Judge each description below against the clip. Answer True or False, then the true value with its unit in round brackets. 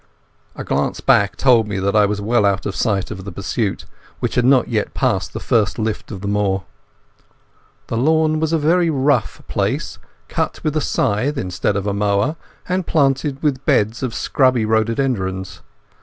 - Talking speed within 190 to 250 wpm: False (180 wpm)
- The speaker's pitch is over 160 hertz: False (110 Hz)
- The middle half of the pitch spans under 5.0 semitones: False (5.3 semitones)